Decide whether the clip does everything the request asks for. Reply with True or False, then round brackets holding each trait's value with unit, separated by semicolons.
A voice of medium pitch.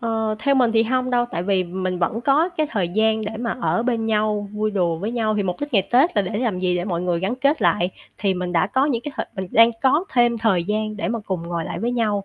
False (215 Hz)